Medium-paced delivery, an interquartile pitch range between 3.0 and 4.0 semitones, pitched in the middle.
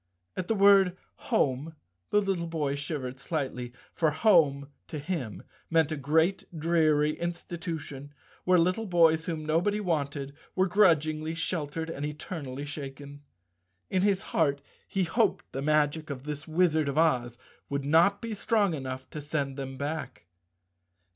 Yes: average, 145 wpm; average, 3.4 semitones; medium, 155 Hz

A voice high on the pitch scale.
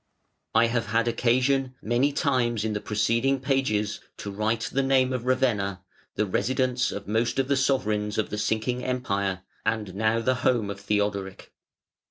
No: low, 115 Hz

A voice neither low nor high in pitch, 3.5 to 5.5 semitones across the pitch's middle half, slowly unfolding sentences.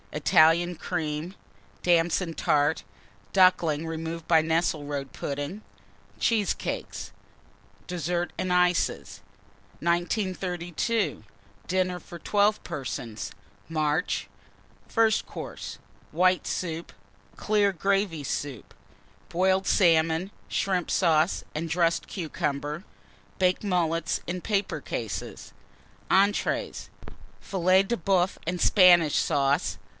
No: medium, 175 Hz; average, 2.8 semitones; slow, 90 wpm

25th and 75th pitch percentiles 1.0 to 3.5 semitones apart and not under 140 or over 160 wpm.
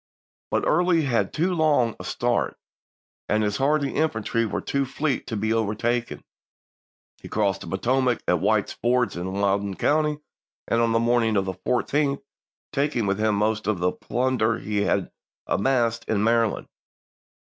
No: average, 4.3 semitones; average, 155 wpm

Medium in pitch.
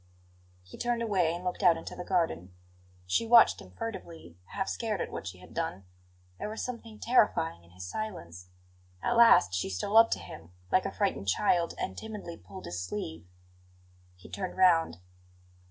Yes: medium, 170 Hz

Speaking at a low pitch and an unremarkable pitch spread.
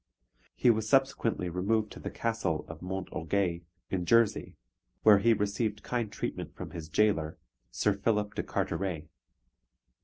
Yes: low, 100 Hz; average, 3.8 semitones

